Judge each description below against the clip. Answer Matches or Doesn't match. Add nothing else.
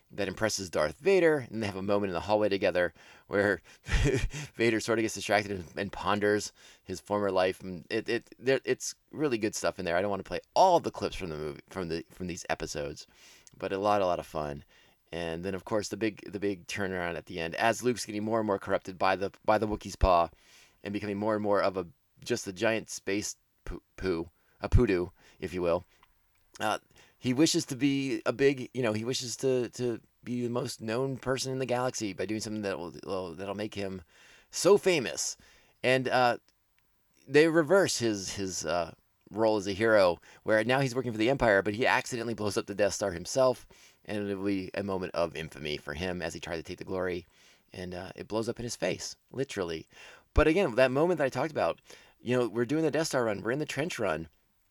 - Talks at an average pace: Doesn't match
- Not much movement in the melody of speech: Doesn't match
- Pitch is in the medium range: Doesn't match